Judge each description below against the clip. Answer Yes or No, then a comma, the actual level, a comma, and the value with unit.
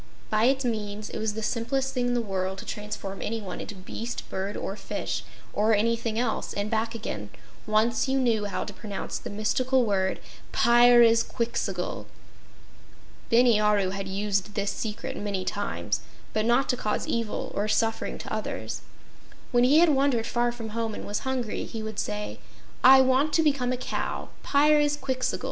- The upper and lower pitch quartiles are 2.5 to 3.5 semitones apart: Yes, average, 3.2 semitones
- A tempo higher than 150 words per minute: Yes, average, 170 wpm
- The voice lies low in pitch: No, high, 225 Hz